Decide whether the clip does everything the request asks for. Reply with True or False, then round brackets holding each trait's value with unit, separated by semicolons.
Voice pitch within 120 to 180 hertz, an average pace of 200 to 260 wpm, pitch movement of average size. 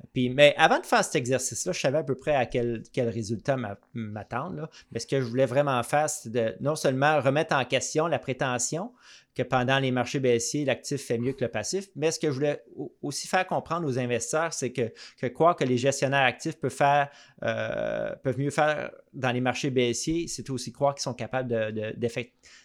True (135 Hz; 215 wpm; 3.6 semitones)